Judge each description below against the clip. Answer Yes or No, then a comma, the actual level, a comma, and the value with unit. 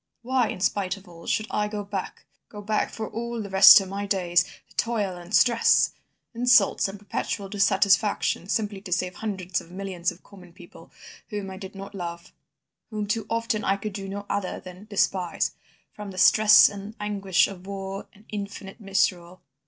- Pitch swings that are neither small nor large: No, narrow, 1.9 semitones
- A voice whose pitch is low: No, high, 200 Hz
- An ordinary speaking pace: Yes, average, 185 wpm